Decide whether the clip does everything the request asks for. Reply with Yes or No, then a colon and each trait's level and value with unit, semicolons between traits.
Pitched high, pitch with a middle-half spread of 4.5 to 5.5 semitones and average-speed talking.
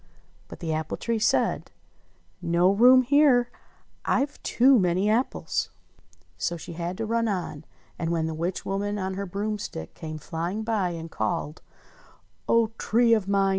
Yes: high, 195 Hz; average, 5.1 semitones; average, 155 wpm